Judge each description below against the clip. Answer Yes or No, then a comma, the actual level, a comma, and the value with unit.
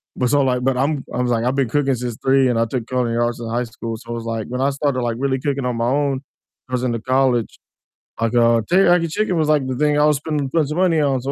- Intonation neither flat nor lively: Yes, average, 3.3 semitones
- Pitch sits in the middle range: No, low, 130 Hz